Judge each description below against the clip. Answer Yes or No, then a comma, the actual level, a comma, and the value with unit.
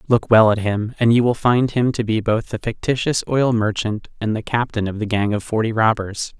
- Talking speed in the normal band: No, fast, 235 wpm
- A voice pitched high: No, low, 110 Hz